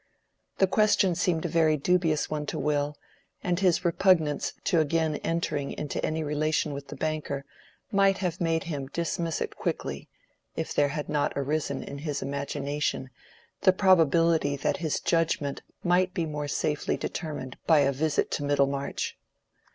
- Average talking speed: Yes, average, 155 wpm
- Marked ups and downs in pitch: No, average, 2.8 semitones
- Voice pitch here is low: No, medium, 155 Hz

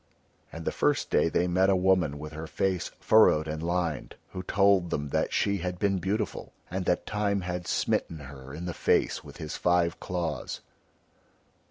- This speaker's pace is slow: No, average, 180 wpm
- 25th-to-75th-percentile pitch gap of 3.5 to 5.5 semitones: No, average, 3.1 semitones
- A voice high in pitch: No, very low, 90 Hz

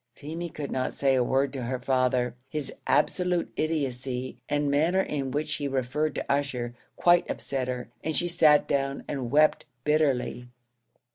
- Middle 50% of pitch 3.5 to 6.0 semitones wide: No, average, 3.1 semitones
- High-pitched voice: No, medium, 140 Hz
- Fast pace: No, average, 165 wpm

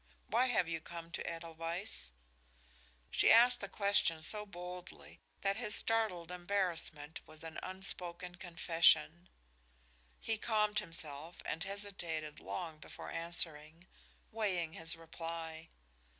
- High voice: No, medium, 175 Hz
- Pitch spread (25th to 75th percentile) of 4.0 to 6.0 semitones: No, average, 3.4 semitones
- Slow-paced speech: Yes, slow, 115 wpm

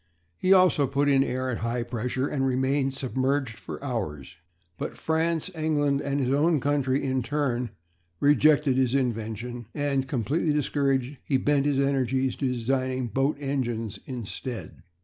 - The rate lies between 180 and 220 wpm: No, average, 150 wpm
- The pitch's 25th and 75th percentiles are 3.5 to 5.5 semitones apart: No, narrow, 2.5 semitones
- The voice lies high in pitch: No, low, 135 Hz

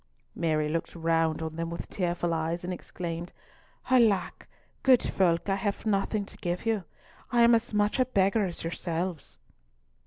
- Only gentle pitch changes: No, average, 3.8 semitones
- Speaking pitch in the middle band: Yes, medium, 180 Hz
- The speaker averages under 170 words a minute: Yes, average, 160 wpm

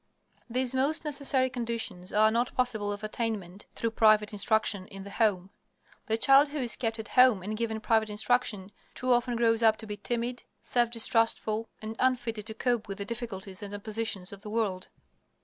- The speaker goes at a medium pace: Yes, average, 185 wpm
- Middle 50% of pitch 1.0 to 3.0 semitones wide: Yes, narrow, 2.6 semitones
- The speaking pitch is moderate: No, high, 225 Hz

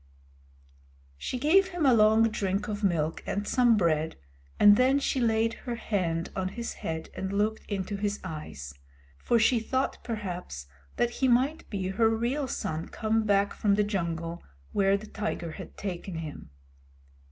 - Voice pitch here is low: No, high, 205 Hz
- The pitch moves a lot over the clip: No, average, 4.1 semitones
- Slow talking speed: No, average, 165 wpm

